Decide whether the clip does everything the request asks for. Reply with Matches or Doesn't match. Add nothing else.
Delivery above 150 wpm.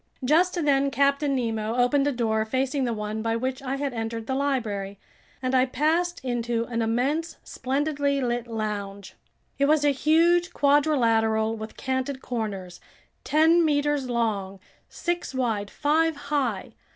Doesn't match